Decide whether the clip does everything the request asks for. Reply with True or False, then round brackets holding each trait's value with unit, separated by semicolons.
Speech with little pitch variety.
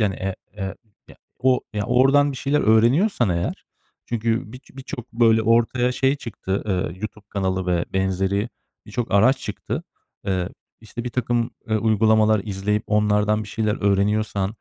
False (3.2 semitones)